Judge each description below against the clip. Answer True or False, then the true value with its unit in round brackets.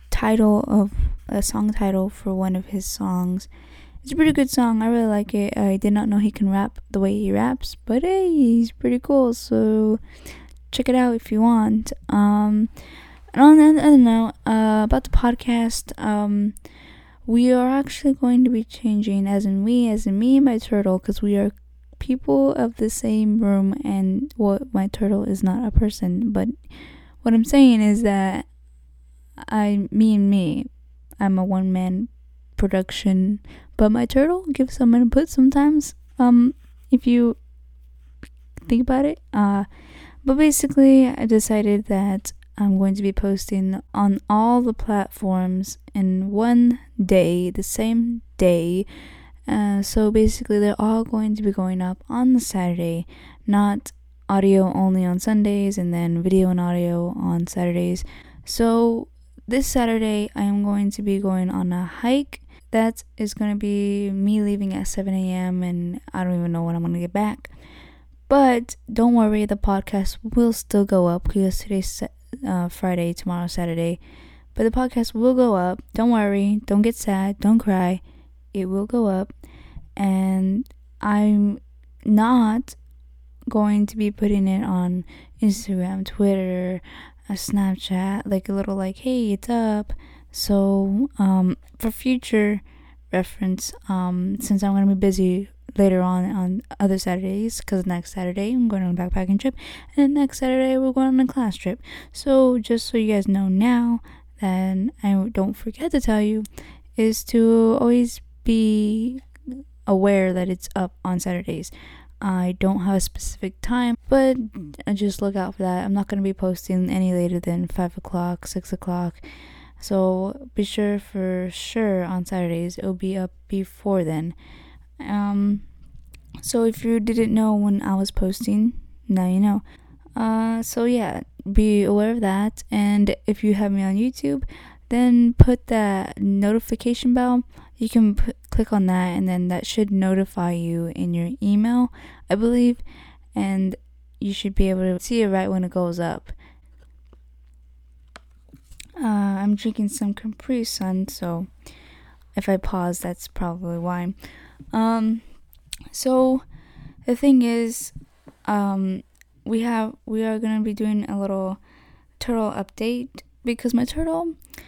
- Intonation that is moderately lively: True (3.6 semitones)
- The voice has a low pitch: False (205 Hz)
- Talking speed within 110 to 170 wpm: True (160 wpm)